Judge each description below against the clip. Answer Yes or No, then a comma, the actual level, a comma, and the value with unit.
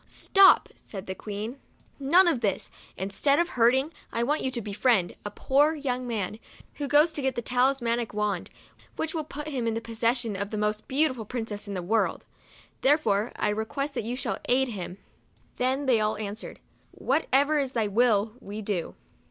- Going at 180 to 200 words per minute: Yes, average, 195 wpm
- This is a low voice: No, high, 235 Hz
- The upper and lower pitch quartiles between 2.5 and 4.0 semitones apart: No, average, 4.6 semitones